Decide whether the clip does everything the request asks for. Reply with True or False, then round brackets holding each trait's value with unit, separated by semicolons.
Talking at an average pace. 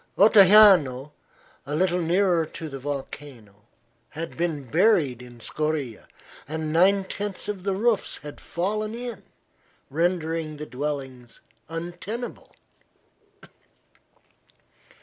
False (100 wpm)